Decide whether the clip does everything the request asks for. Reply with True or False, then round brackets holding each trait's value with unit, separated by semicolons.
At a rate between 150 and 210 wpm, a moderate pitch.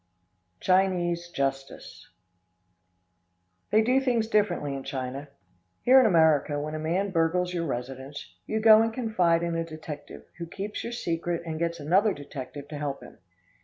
True (155 wpm; 170 Hz)